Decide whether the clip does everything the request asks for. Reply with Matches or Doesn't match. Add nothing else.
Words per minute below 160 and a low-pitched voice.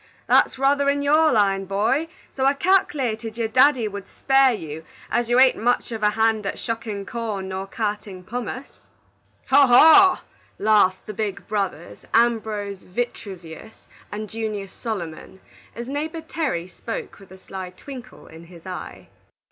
Doesn't match